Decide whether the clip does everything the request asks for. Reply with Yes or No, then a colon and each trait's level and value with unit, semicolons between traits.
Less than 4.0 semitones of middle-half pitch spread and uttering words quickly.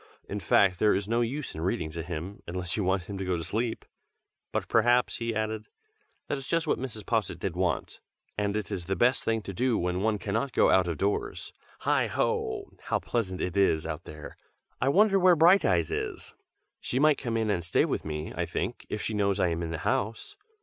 No: average, 4.6 semitones; fast, 220 wpm